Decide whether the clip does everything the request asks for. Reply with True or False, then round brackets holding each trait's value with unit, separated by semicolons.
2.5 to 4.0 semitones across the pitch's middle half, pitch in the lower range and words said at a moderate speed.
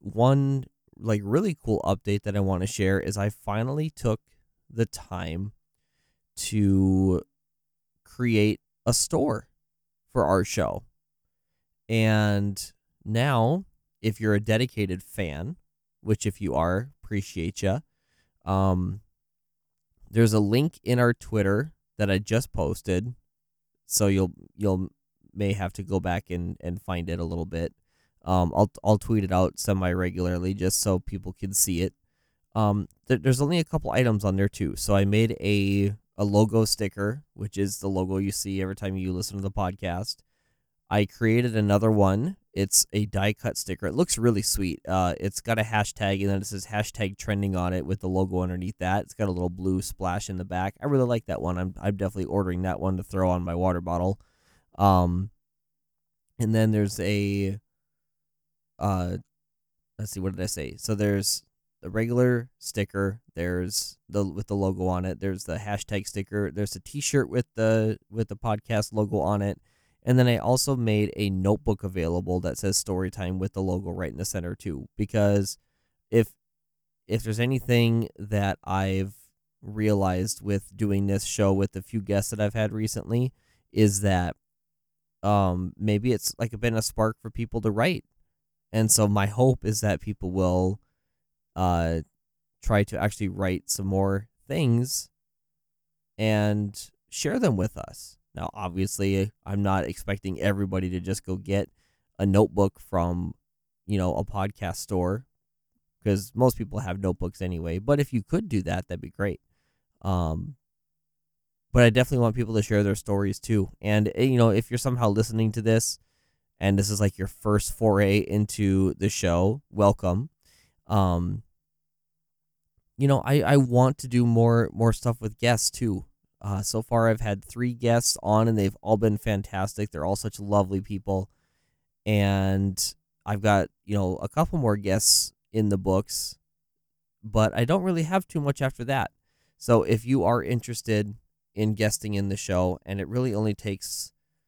True (3.3 semitones; 100 Hz; 170 wpm)